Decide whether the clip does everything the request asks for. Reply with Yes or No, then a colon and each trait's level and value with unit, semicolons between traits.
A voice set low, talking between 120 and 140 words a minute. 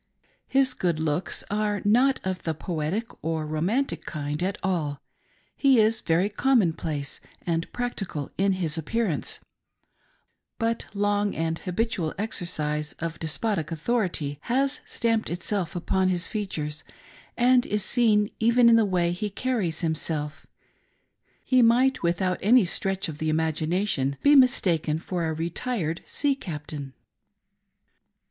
No: medium, 185 Hz; slow, 135 wpm